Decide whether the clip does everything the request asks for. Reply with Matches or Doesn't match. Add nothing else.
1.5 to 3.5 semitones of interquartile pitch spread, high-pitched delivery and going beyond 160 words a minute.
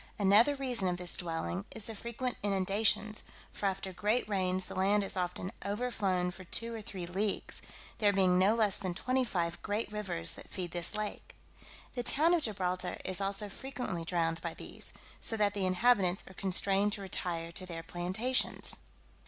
Matches